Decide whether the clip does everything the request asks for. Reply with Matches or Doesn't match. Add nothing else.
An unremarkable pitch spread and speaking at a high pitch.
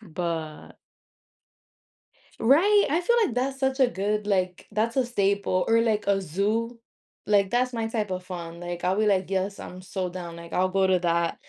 Matches